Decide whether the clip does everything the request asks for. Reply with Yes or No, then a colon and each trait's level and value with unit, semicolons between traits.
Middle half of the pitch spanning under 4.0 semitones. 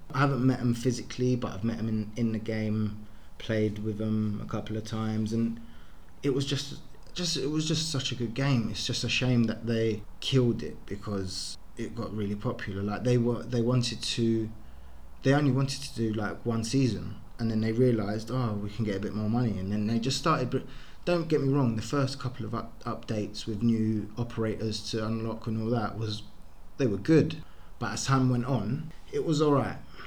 Yes: average, 2.9 semitones